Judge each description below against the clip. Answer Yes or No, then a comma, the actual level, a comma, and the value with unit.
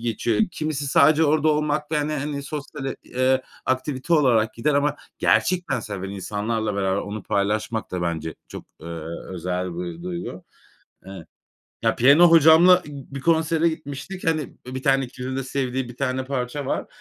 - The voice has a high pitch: No, low, 135 Hz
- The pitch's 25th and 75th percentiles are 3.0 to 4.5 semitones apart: No, average, 5.3 semitones